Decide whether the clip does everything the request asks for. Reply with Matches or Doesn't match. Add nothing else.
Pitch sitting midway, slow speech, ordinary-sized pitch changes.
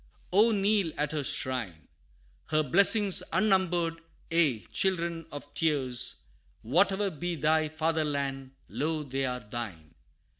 Matches